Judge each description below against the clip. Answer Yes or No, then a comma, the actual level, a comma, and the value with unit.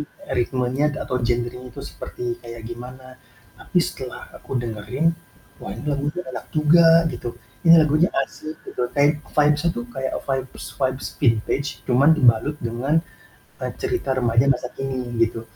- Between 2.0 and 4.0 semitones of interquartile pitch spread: Yes, average, 3.7 semitones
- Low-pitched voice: Yes, low, 130 Hz